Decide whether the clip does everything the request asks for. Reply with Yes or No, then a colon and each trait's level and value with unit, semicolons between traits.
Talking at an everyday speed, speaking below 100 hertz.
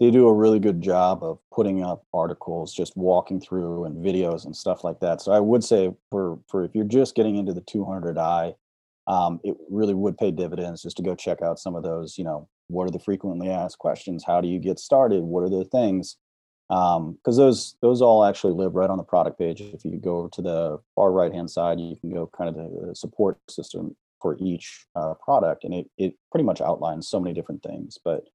No: fast, 235 wpm; very low, 90 Hz